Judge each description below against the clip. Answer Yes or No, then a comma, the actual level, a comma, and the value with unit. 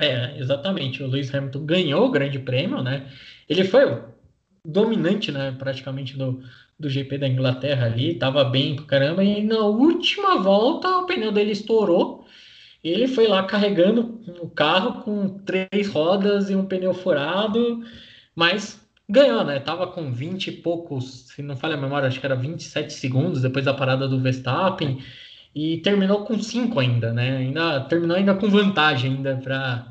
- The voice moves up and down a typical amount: No, wide, 6.8 semitones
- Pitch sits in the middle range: Yes, medium, 160 Hz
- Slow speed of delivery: No, average, 170 wpm